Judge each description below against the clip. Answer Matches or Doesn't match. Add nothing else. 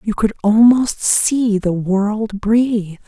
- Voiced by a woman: Matches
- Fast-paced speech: Doesn't match